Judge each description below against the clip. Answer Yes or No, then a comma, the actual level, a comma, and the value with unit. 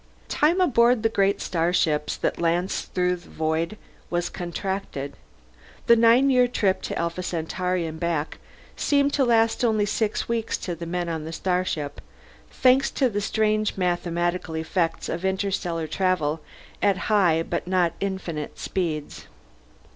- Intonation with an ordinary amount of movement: Yes, average, 4.3 semitones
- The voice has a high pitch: No, medium, 180 Hz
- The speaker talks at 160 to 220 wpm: No, average, 145 wpm